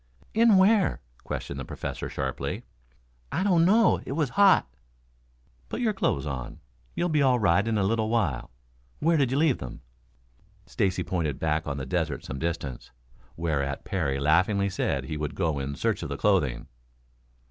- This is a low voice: Yes, very low, 95 Hz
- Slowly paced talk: No, average, 170 wpm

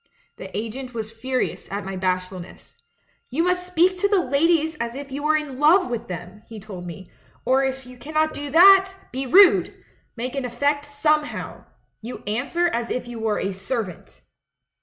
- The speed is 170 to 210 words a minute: Yes, average, 180 wpm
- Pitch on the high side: Yes, very high, 260 Hz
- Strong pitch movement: Yes, wide, 5.8 semitones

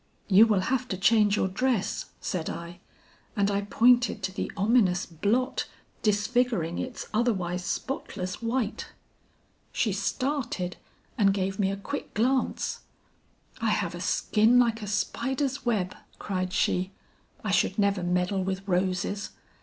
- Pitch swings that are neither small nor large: Yes, average, 4.3 semitones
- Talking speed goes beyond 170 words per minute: No, average, 140 wpm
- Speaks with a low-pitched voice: No, high, 205 Hz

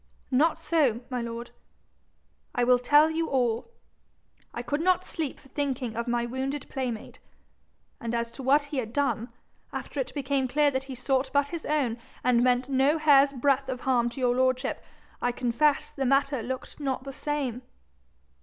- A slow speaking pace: No, average, 175 wpm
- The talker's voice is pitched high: Yes, very high, 265 Hz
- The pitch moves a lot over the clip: No, average, 2.7 semitones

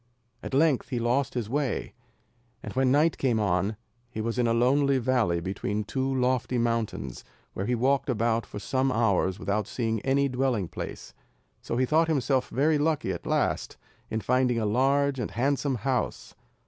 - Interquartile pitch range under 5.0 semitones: Yes, average, 3.3 semitones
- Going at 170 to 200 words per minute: Yes, average, 175 wpm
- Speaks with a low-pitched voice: Yes, low, 125 Hz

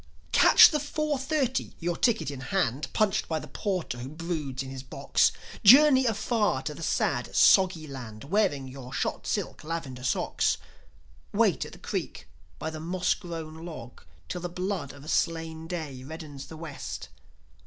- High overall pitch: No, medium, 160 Hz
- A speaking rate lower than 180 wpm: Yes, average, 165 wpm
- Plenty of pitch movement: Yes, wide, 5.8 semitones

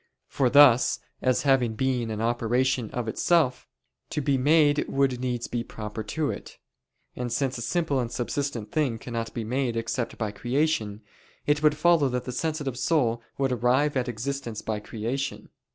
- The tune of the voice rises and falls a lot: No, average, 3.2 semitones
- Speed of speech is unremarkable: Yes, average, 170 wpm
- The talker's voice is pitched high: No, low, 125 Hz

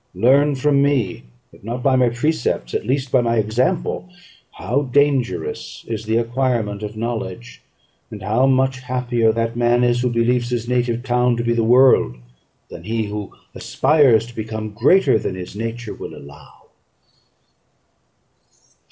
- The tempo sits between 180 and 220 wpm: No, average, 150 wpm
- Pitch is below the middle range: Yes, low, 120 Hz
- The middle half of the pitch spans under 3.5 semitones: Yes, narrow, 2.6 semitones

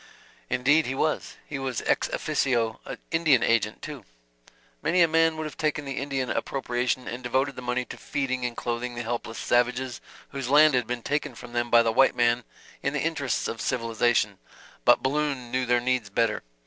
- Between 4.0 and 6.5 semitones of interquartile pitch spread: No, average, 2.8 semitones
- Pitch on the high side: No, low, 125 Hz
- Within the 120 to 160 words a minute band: No, average, 185 wpm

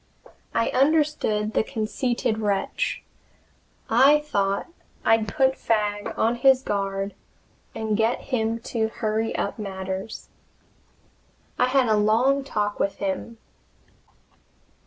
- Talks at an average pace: No, slow, 110 wpm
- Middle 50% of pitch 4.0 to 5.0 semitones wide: No, average, 3.5 semitones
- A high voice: Yes, high, 220 Hz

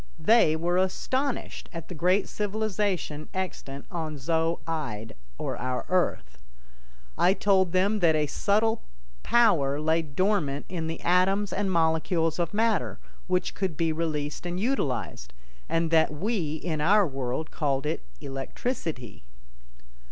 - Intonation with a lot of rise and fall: No, average, 4.4 semitones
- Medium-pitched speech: Yes, medium, 165 Hz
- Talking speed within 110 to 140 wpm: Yes, slow, 135 wpm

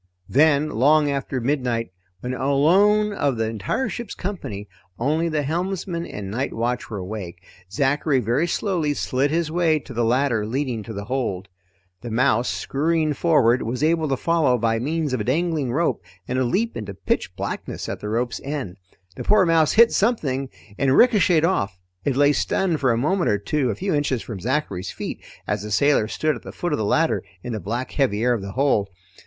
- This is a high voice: No, low, 135 Hz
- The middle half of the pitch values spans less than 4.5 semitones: No, wide, 5.6 semitones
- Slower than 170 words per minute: No, average, 195 wpm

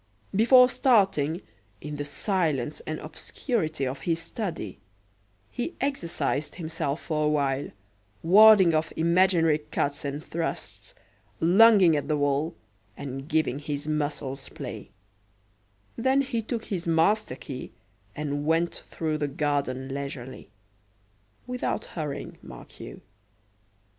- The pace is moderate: No, slow, 120 wpm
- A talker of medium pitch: Yes, medium, 155 Hz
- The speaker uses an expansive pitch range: No, average, 4.7 semitones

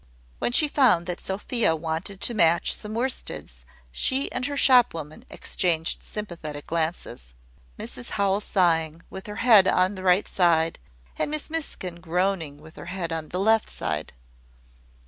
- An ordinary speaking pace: Yes, average, 155 wpm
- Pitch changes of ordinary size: Yes, average, 4.7 semitones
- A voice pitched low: No, medium, 180 Hz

